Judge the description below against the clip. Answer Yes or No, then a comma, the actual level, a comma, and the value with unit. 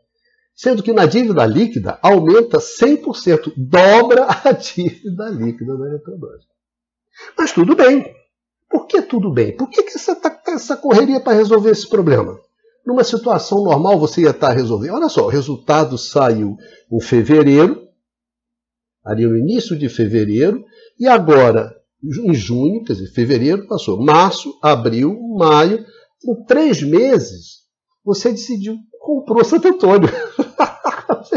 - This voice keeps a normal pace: Yes, average, 140 wpm